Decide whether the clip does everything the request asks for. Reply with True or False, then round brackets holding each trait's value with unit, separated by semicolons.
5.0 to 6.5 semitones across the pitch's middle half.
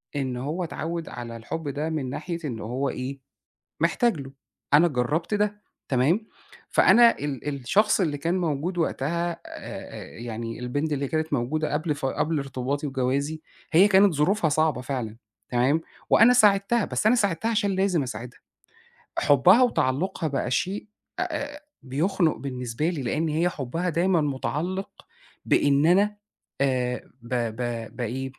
True (5.3 semitones)